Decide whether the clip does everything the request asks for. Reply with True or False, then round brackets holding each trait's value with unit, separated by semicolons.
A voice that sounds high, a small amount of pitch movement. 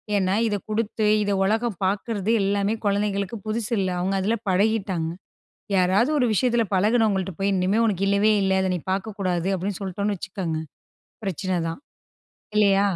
True (200 Hz; 2.2 semitones)